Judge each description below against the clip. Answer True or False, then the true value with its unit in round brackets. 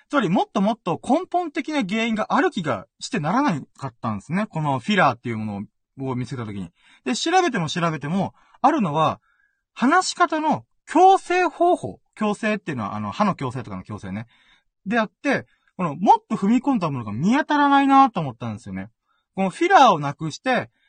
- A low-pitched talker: False (200 Hz)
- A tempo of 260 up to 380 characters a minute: False (390 characters per minute)